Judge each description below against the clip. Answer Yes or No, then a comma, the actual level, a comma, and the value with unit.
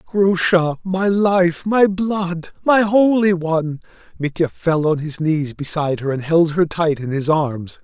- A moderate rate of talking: Yes, average, 170 wpm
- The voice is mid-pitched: Yes, medium, 170 Hz